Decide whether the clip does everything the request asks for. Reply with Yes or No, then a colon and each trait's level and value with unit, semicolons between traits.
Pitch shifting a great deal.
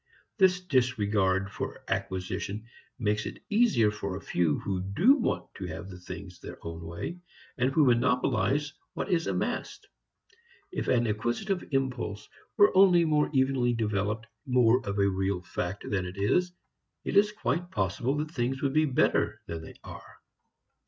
Yes: wide, 7.0 semitones